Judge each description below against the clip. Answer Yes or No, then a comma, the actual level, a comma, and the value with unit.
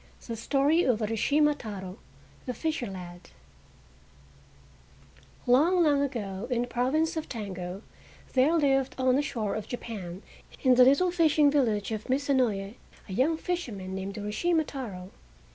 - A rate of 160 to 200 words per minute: No, average, 145 wpm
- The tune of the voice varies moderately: No, wide, 5.9 semitones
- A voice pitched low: No, very high, 250 Hz